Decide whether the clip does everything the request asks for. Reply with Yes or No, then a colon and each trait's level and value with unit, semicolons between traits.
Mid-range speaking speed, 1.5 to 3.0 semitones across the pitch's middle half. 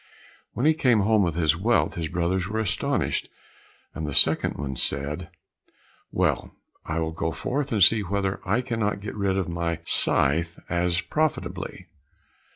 No: average, 155 wpm; average, 4.7 semitones